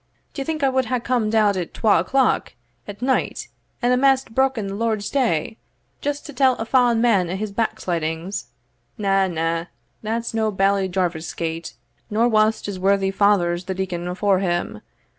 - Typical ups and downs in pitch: Yes, average, 4.5 semitones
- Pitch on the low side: No, high, 205 Hz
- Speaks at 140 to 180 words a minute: Yes, average, 170 wpm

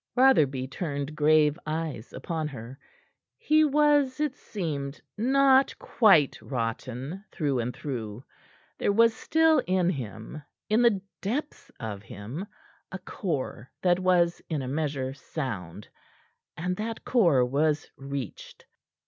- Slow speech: Yes, slow, 125 wpm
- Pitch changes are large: Yes, wide, 8.2 semitones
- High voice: No, medium, 155 Hz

